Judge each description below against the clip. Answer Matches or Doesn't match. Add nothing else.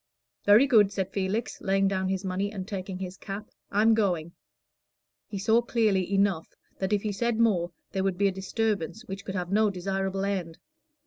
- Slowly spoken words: Doesn't match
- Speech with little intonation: Matches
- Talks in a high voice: Matches